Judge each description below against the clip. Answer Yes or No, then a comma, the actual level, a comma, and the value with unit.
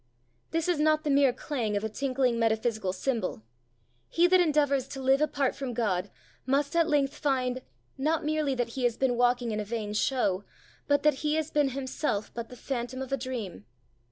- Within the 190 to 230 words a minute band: Yes, average, 195 wpm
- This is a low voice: No, very high, 265 Hz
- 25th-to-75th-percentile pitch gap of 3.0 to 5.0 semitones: Yes, average, 3.8 semitones